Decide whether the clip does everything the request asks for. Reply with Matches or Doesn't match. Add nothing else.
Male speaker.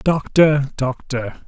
Matches